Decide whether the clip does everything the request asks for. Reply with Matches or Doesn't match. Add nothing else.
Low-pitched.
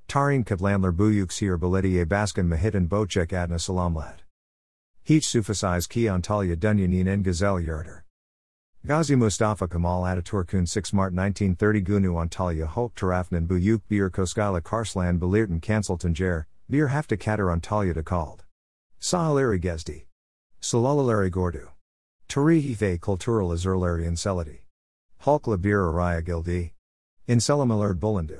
Matches